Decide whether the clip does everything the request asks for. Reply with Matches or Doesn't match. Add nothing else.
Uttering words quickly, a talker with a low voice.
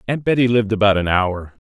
Matches